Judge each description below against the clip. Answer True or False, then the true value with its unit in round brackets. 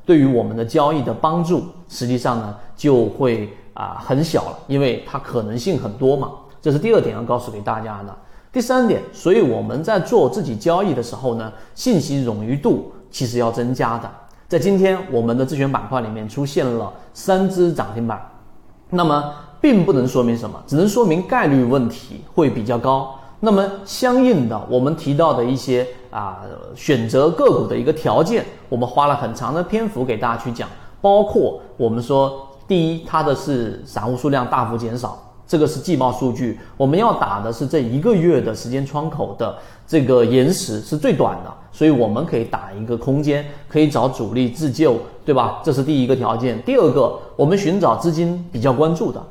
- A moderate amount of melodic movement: True (5.0 semitones)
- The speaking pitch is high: False (130 Hz)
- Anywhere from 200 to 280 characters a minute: False (290 characters per minute)